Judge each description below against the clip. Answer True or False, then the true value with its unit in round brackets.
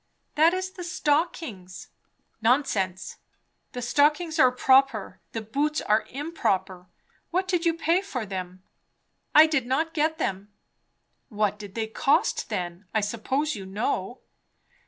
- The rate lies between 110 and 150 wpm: True (135 wpm)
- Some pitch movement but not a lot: False (7.5 semitones)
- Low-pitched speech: False (255 Hz)